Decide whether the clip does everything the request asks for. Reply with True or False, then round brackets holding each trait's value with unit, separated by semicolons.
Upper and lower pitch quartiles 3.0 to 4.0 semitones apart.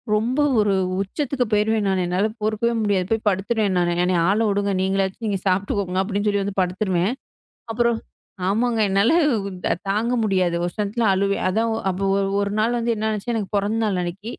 False (2.5 semitones)